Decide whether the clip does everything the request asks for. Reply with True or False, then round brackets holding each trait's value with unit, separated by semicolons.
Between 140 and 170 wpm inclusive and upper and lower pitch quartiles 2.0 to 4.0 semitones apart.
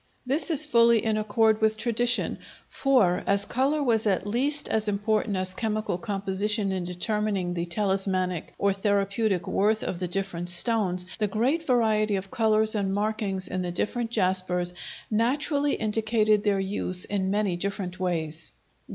True (150 wpm; 2.9 semitones)